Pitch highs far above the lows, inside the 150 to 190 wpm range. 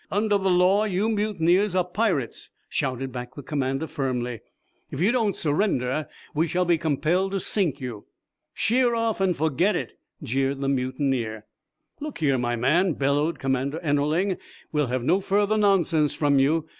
Yes: wide, 6.2 semitones; average, 160 wpm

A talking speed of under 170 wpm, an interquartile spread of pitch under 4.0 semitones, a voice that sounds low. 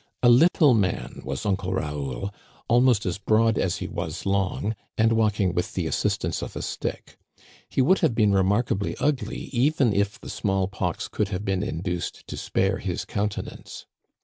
No: average, 175 wpm; average, 3.2 semitones; low, 100 Hz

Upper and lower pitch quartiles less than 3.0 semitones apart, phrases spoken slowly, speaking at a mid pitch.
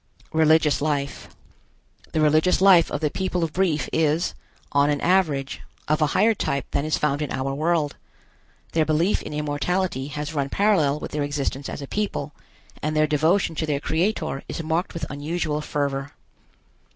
No: narrow, 2.5 semitones; average, 170 wpm; medium, 155 Hz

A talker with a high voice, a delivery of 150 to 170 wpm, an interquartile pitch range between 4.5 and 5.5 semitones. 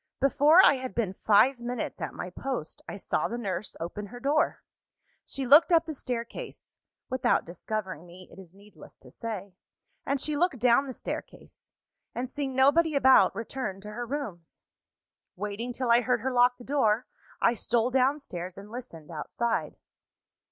Yes: high, 240 Hz; average, 165 wpm; average, 4.8 semitones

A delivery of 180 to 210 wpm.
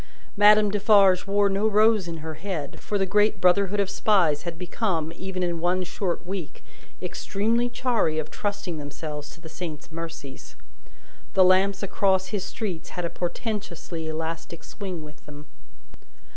No: average, 155 wpm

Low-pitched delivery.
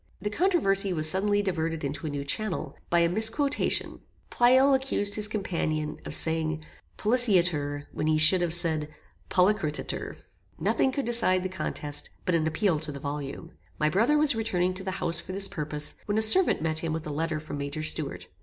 No: medium, 175 Hz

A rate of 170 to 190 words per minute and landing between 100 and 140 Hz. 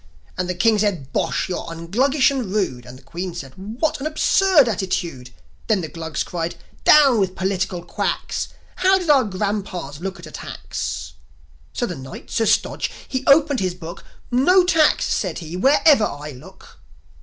No: average, 175 wpm; high, 190 Hz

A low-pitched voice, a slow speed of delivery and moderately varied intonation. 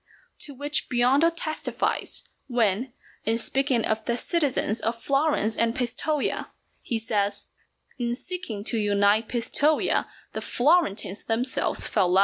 No: high, 240 Hz; slow, 130 wpm; average, 4.7 semitones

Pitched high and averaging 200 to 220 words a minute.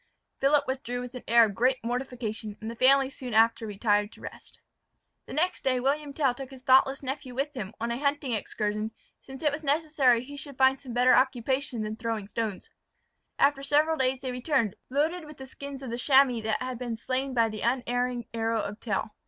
Yes: very high, 255 Hz; fast, 205 wpm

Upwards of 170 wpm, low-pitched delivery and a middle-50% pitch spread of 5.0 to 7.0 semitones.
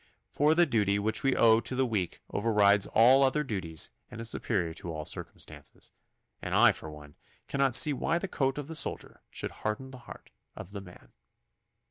Yes: average, 190 wpm; low, 115 Hz; wide, 5.5 semitones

